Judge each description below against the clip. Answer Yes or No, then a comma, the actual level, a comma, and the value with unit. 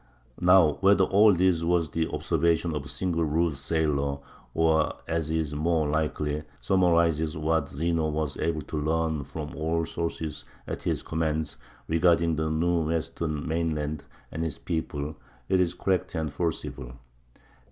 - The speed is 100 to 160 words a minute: Yes, average, 145 wpm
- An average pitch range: No, narrow, 1.6 semitones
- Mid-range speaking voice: No, very low, 80 Hz